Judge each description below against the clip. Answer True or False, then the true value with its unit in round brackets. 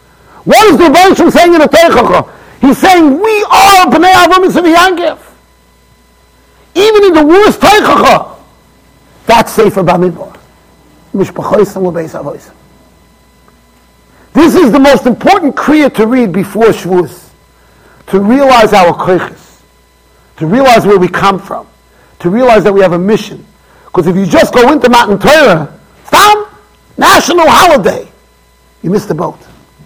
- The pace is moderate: False (130 wpm)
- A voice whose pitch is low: False (250 Hz)